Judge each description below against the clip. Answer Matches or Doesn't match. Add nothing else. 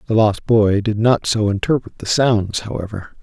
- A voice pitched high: Doesn't match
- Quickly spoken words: Doesn't match